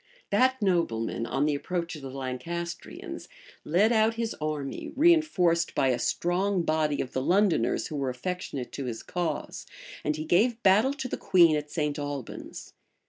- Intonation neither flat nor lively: No, wide, 5.8 semitones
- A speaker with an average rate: Yes, average, 165 wpm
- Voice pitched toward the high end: No, medium, 170 Hz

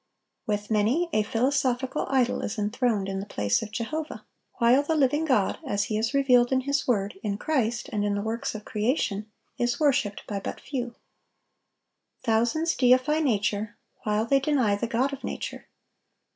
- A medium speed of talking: Yes, average, 170 wpm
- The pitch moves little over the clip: No, average, 4.4 semitones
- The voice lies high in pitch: Yes, high, 235 Hz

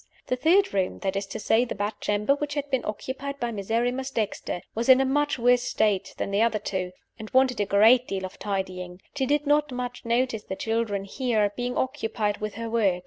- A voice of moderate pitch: No, high, 230 Hz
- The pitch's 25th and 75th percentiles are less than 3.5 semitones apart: No, average, 4.3 semitones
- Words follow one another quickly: Yes, fast, 210 wpm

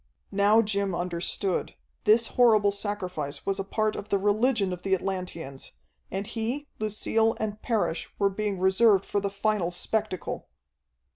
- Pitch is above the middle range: Yes, high, 200 Hz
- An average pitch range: No, narrow, 2.3 semitones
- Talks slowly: No, average, 145 wpm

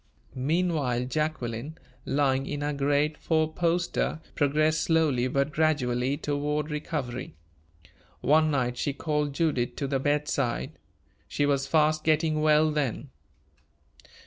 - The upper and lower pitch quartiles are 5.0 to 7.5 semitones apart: No, narrow, 2.4 semitones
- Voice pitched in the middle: Yes, medium, 145 Hz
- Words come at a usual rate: No, slow, 120 wpm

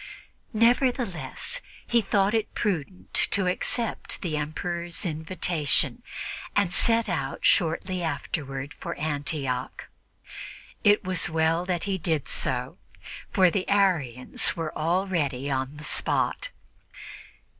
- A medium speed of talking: No, slow, 110 wpm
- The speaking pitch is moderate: Yes, medium, 170 Hz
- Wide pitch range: No, average, 4.4 semitones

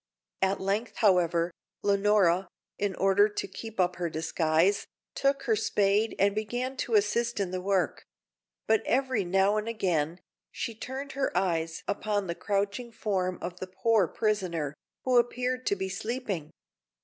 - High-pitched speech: Yes, high, 200 Hz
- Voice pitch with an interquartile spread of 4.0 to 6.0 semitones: No, average, 3.5 semitones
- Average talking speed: Yes, average, 150 wpm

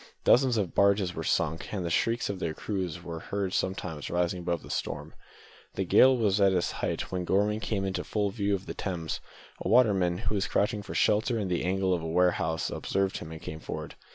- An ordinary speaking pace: No, fast, 215 wpm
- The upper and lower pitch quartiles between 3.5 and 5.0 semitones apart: No, average, 2.9 semitones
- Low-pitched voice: Yes, very low, 95 Hz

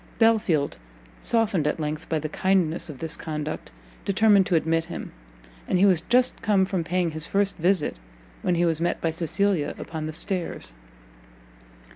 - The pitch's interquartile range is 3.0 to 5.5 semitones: Yes, average, 3.9 semitones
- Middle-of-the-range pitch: Yes, medium, 170 Hz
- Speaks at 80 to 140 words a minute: No, average, 165 wpm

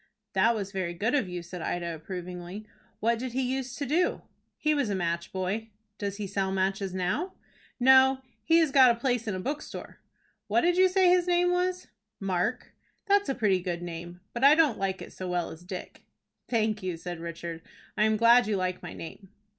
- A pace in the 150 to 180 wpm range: No, fast, 205 wpm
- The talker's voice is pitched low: No, high, 210 Hz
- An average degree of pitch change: No, wide, 6.6 semitones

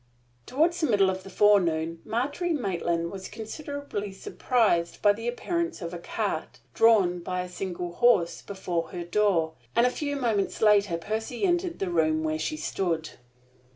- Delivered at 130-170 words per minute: Yes, average, 160 wpm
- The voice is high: Yes, high, 200 Hz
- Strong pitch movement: Yes, wide, 5.8 semitones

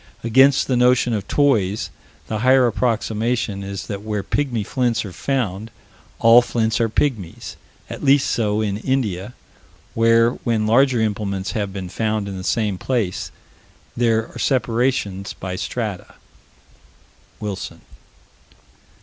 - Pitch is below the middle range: Yes, low, 110 Hz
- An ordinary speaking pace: No, slow, 130 wpm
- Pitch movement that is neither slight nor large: Yes, average, 3.5 semitones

